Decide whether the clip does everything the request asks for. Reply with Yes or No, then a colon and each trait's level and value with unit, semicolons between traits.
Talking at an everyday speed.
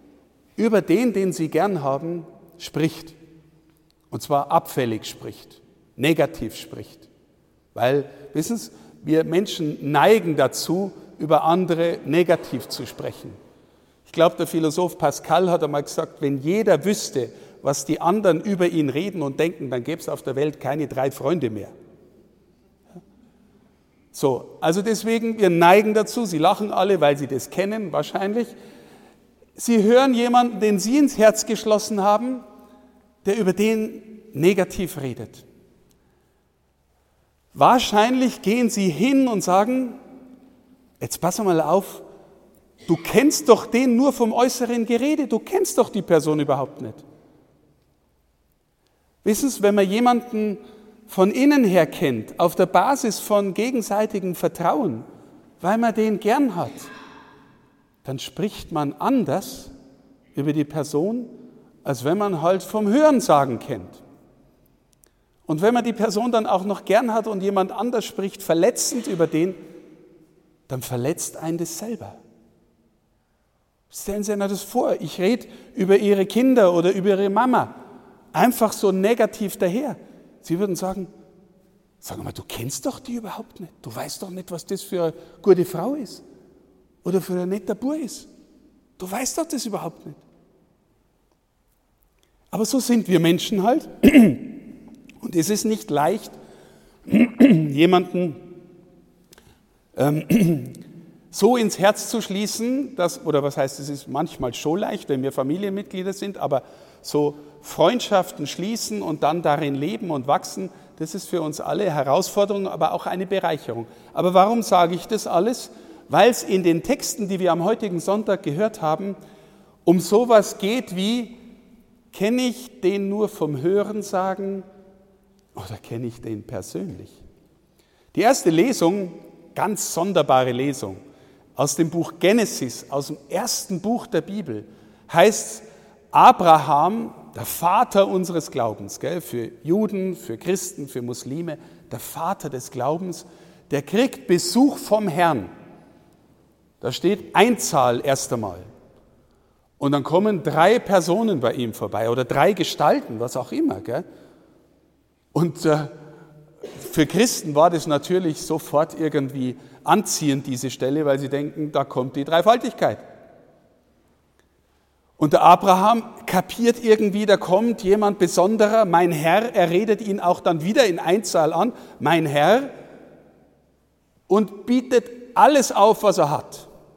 Yes: average, 135 wpm